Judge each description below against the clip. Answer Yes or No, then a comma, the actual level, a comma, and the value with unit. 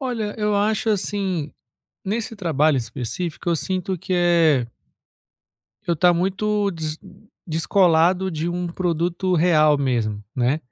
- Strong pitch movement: No, average, 3.7 semitones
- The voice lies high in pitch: No, medium, 175 Hz